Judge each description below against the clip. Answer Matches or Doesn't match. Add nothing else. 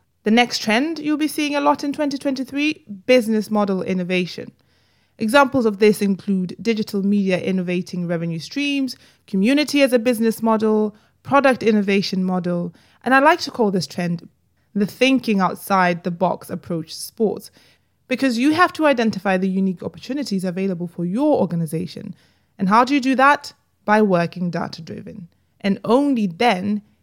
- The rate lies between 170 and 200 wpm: Doesn't match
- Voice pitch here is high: Matches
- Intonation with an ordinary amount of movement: Doesn't match